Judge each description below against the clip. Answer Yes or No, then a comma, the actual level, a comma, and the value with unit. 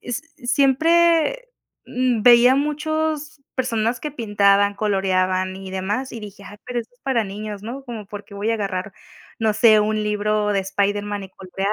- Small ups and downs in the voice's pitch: No, average, 4.2 semitones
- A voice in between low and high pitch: No, high, 215 Hz